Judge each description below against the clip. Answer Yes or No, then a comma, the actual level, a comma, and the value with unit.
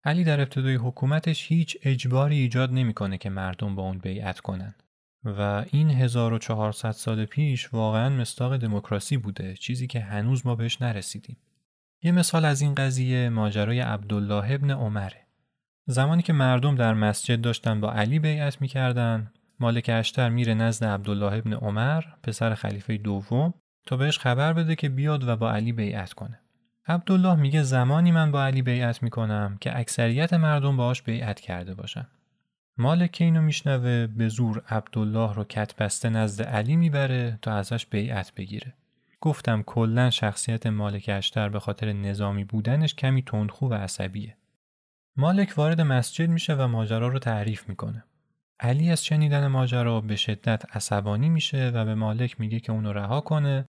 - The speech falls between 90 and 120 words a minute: No, fast, 155 wpm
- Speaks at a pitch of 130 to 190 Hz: No, low, 120 Hz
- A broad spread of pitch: No, average, 4.5 semitones